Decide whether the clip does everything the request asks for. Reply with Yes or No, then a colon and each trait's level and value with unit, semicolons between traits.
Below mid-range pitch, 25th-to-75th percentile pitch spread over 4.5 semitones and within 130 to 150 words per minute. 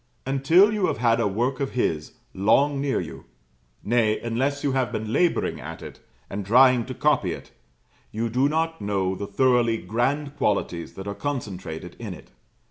No: low, 120 Hz; average, 5.2 semitones; average, 175 wpm